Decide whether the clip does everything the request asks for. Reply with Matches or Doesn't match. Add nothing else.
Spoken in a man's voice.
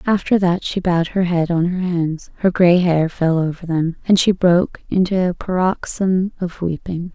Doesn't match